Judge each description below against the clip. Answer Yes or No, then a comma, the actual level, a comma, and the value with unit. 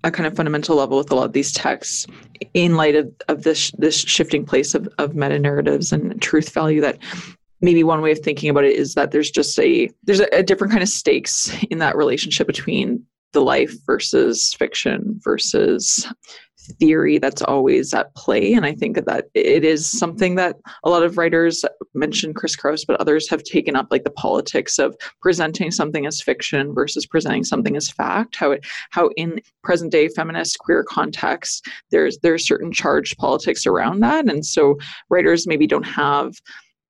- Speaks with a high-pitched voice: No, medium, 165 Hz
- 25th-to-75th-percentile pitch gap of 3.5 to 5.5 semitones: Yes, average, 5.2 semitones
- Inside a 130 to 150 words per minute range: No, average, 185 wpm